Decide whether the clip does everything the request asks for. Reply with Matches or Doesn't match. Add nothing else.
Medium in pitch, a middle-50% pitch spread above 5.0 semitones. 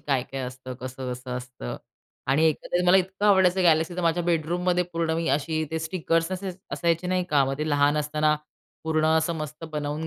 Doesn't match